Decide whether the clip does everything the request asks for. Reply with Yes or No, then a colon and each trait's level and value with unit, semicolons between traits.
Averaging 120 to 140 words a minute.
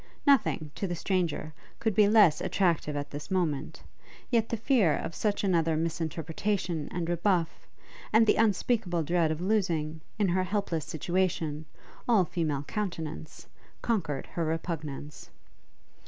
Yes: slow, 135 wpm